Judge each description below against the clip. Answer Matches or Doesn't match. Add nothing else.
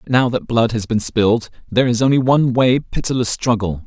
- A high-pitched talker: Doesn't match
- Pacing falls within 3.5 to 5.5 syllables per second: Doesn't match